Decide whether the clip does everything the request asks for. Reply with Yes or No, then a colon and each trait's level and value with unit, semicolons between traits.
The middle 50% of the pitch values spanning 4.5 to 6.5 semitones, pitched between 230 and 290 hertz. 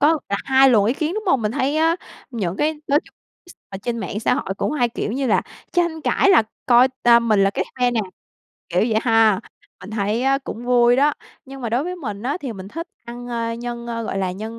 No: average, 4.1 semitones; high, 240 Hz